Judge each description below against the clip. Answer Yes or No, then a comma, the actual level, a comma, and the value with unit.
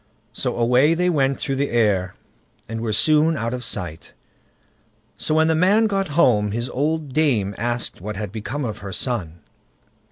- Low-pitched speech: Yes, low, 125 Hz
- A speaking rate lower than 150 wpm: No, average, 170 wpm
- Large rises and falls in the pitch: Yes, wide, 6.4 semitones